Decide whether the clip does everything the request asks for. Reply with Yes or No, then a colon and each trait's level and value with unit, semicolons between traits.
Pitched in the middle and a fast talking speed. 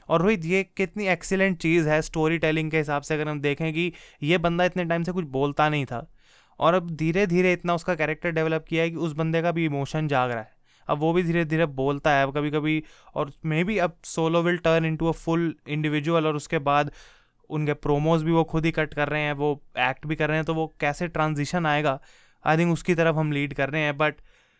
Yes: medium, 160 Hz; fast, 240 wpm